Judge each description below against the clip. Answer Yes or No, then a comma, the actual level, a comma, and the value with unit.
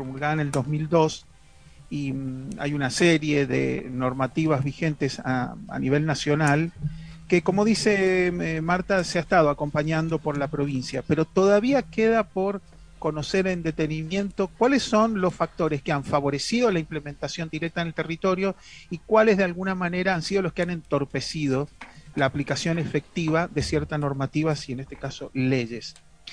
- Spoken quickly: No, average, 155 wpm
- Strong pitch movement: No, average, 4.2 semitones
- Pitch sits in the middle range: Yes, medium, 160 Hz